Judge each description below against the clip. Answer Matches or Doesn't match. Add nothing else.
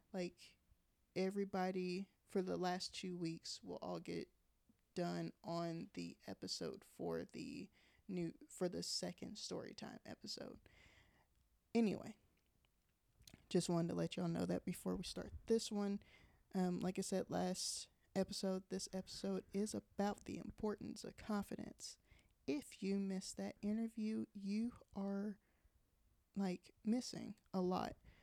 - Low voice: Doesn't match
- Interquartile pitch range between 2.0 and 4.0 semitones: Matches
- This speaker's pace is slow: Matches